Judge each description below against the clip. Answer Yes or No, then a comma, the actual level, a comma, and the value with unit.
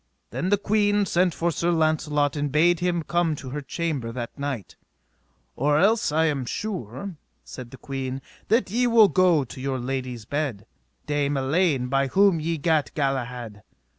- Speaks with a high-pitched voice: No, medium, 150 Hz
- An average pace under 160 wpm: No, average, 165 wpm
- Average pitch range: Yes, average, 4.8 semitones